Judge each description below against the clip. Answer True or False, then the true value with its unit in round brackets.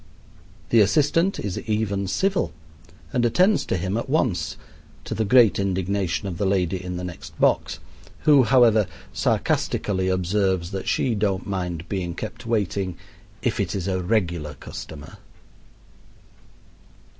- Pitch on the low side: True (100 Hz)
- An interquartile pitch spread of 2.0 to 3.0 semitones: False (3.8 semitones)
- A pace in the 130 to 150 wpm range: True (135 wpm)